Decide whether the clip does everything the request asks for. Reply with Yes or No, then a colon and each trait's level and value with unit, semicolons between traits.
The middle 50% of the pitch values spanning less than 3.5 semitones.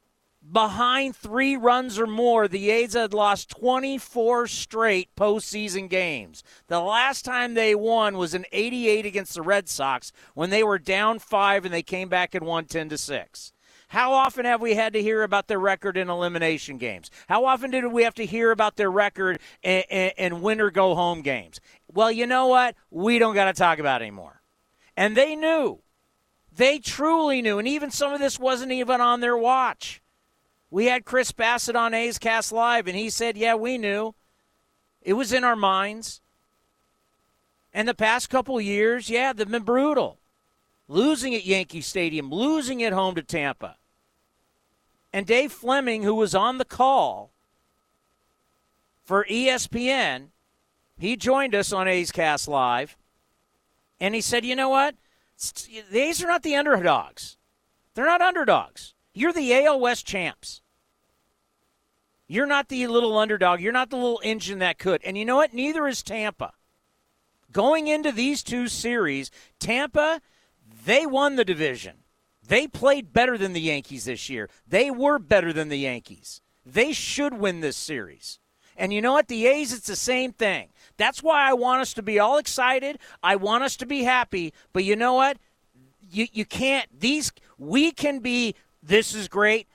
No: average, 5.3 semitones